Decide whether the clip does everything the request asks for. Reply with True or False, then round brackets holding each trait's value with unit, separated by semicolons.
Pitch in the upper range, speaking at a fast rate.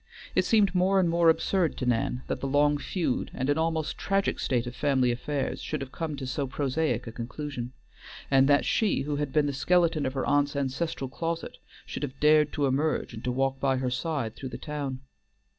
False (145 Hz; 210 wpm)